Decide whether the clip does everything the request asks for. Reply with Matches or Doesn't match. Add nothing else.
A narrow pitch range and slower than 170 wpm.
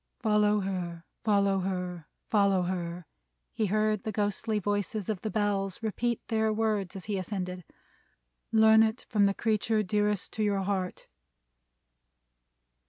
Matches